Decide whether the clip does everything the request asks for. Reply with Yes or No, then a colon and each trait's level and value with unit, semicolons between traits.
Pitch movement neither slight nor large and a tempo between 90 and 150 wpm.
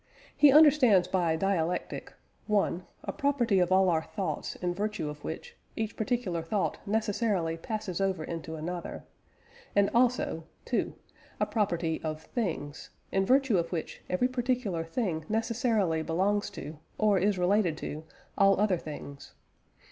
Yes: average, 5.0 semitones; average, 140 wpm